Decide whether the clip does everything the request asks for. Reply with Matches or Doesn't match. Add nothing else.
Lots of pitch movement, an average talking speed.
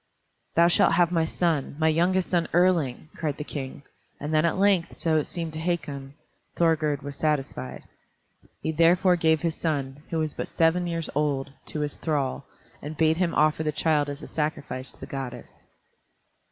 Doesn't match